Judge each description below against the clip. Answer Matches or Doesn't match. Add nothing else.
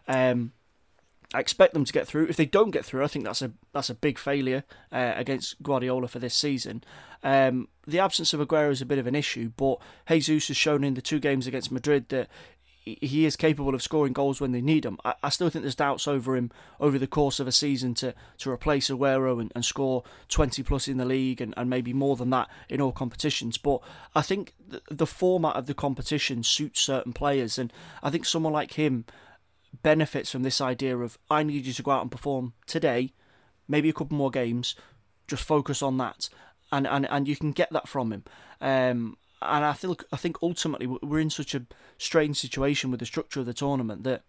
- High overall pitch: Doesn't match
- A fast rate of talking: Matches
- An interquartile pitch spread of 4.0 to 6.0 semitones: Doesn't match